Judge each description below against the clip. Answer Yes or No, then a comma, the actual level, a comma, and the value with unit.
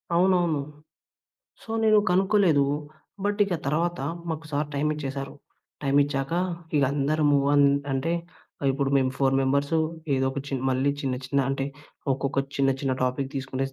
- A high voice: No, medium, 140 Hz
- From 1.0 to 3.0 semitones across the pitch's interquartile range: Yes, average, 2.7 semitones